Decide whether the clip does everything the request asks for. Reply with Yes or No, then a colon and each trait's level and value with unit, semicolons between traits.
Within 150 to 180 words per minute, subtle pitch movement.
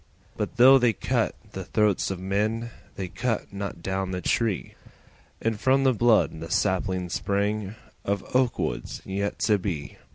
No: average, 160 wpm; average, 3.3 semitones